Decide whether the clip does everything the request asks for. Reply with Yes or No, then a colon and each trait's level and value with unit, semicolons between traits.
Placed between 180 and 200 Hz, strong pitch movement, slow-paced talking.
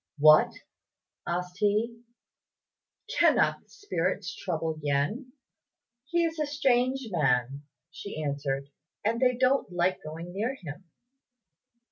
Yes: medium, 185 Hz; wide, 8.7 semitones; slow, 110 wpm